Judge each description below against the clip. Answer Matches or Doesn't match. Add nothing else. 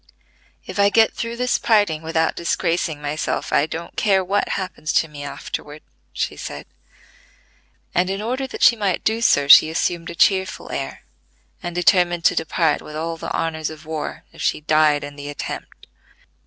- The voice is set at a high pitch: Doesn't match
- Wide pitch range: Doesn't match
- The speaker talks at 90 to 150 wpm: Doesn't match